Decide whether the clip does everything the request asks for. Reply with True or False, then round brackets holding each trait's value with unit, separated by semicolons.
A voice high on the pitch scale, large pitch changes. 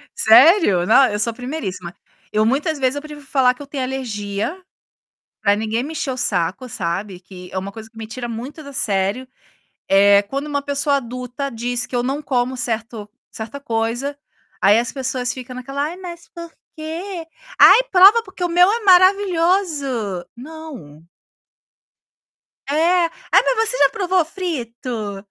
True (255 Hz; 6.1 semitones)